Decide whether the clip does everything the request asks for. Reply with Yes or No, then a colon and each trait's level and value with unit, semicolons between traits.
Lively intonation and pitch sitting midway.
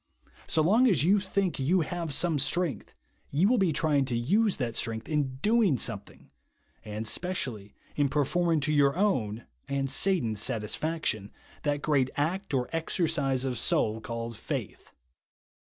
Yes: wide, 6.1 semitones; medium, 145 Hz